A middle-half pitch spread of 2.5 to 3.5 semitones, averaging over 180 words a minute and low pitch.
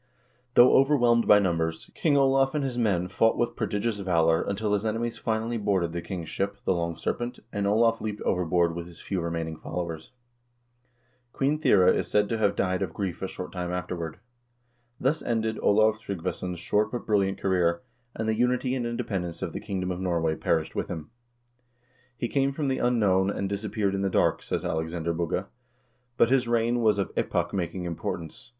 No: average, 4.9 semitones; average, 190 wpm; low, 100 Hz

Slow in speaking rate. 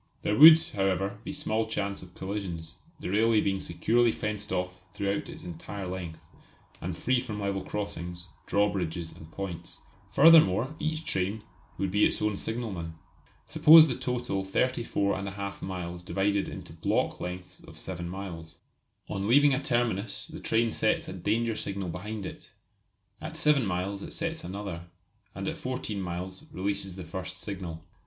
No: average, 155 wpm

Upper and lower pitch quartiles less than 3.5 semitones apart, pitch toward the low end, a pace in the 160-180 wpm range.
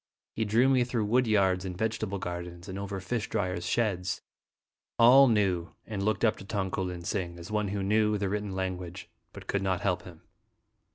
No: average, 2.9 semitones; low, 100 Hz; average, 195 wpm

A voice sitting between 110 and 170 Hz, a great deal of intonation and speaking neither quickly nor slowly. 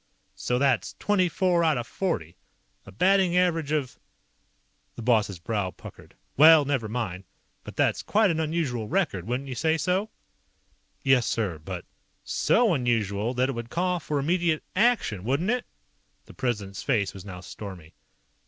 Yes: low, 135 Hz; wide, 8.0 semitones; average, 160 wpm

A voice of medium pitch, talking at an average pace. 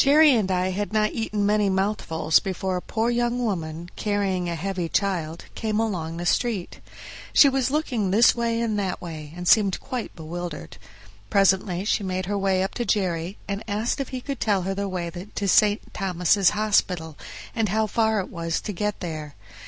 No: high, 195 Hz; average, 190 wpm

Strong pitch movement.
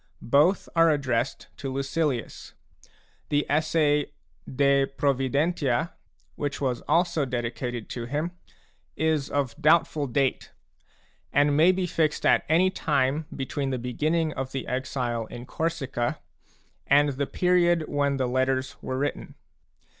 No: average, 3.2 semitones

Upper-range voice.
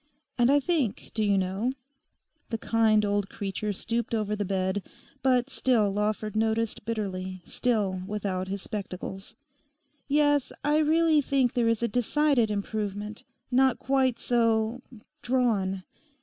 Yes: high, 220 Hz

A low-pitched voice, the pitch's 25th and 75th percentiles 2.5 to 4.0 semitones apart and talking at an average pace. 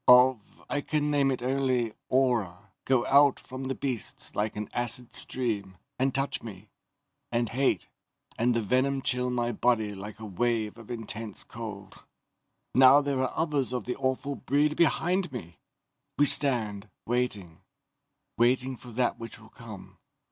Yes: low, 125 Hz; average, 3.4 semitones; average, 155 wpm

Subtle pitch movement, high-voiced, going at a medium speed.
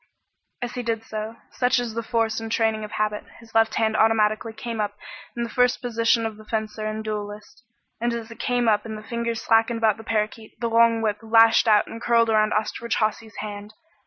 No: narrow, 1.2 semitones; high, 225 Hz; fast, 220 wpm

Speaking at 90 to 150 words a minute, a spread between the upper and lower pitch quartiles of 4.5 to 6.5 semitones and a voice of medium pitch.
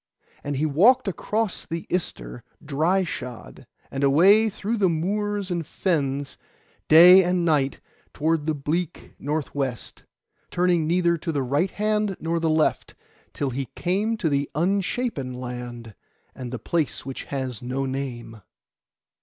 Yes: average, 145 wpm; average, 5.1 semitones; medium, 160 Hz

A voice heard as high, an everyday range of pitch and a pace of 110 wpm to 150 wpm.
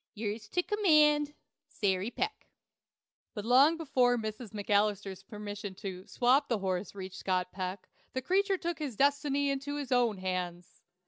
No: high, 225 Hz; wide, 6.7 semitones; average, 145 wpm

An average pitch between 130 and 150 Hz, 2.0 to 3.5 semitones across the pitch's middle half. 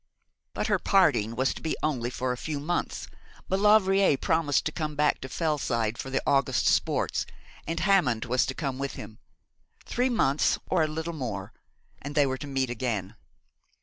No: medium, 140 Hz; average, 4.4 semitones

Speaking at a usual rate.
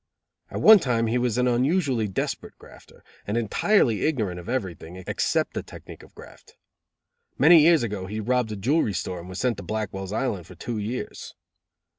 Yes: average, 180 wpm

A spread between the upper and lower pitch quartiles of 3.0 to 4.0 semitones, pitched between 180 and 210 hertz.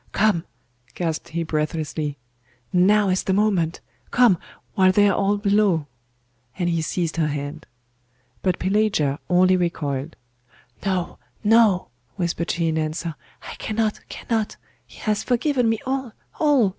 No: average, 4.5 semitones; medium, 185 Hz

